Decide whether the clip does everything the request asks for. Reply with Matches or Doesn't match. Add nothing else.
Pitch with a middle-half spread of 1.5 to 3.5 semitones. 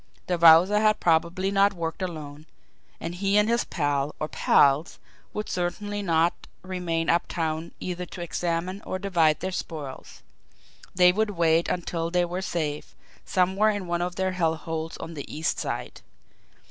Matches